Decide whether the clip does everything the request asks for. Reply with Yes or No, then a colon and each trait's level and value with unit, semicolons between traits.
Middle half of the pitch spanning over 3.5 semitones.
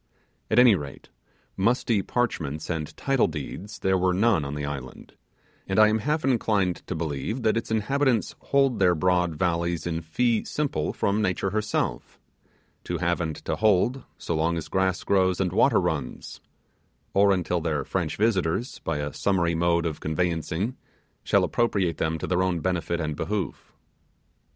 Yes: average, 4.8 semitones